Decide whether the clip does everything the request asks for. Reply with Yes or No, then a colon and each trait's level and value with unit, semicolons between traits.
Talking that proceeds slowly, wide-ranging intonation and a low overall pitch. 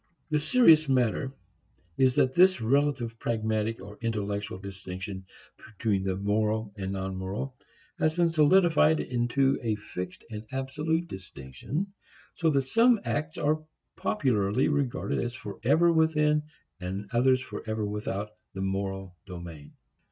Yes: slow, 130 wpm; wide, 7.0 semitones; low, 115 Hz